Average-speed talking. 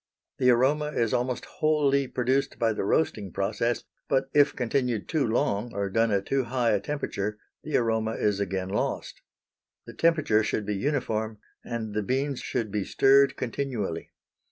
Yes: average, 160 wpm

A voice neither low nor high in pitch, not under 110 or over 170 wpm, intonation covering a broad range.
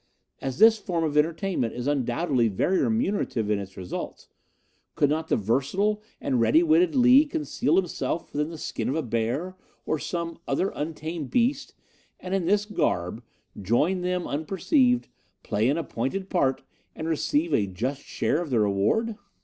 Yes: medium, 160 Hz; average, 160 wpm; wide, 7.5 semitones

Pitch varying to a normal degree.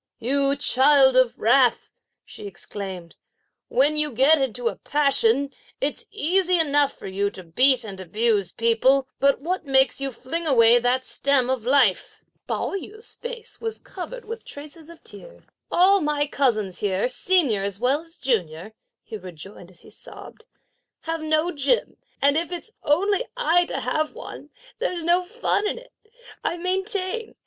No: wide, 6.9 semitones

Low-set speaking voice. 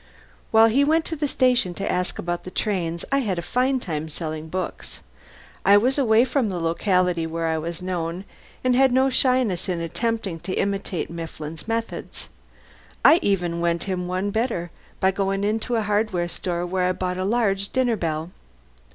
No: high, 190 Hz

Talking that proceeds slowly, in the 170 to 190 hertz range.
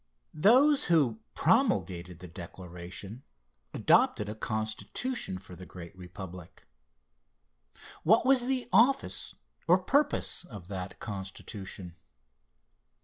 No: slow, 95 wpm; low, 105 Hz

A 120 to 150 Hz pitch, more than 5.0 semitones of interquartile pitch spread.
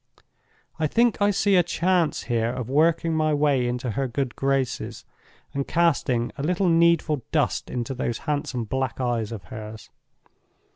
Yes: medium, 140 Hz; wide, 5.5 semitones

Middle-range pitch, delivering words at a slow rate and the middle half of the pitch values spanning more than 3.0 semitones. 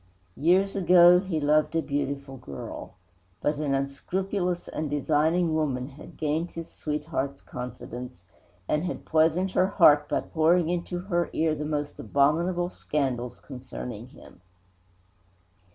Yes: medium, 155 Hz; slow, 130 wpm; average, 3.9 semitones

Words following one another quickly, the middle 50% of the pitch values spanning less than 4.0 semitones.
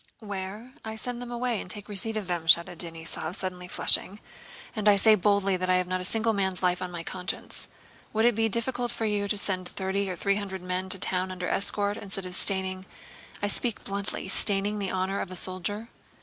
Yes: fast, 210 wpm; narrow, 2.4 semitones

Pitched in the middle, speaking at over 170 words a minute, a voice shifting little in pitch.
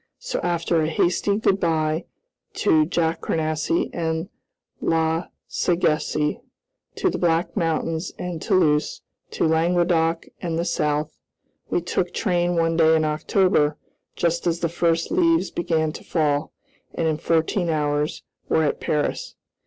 No: medium, 165 Hz; slow, 135 wpm; narrow, 1.7 semitones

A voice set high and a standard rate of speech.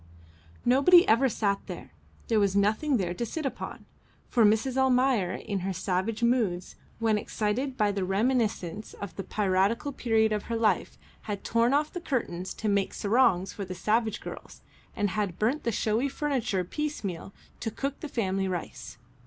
Yes: high, 215 Hz; average, 170 wpm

